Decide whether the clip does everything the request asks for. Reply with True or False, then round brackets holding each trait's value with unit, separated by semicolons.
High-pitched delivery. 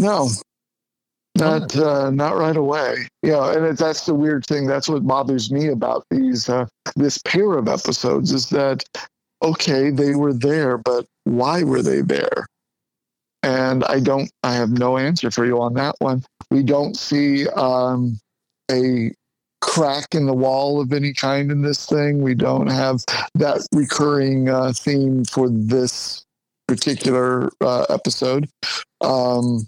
False (135 Hz)